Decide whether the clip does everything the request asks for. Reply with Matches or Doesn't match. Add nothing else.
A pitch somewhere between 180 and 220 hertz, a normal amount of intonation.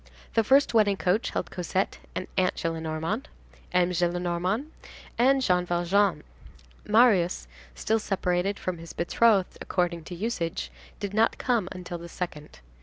Matches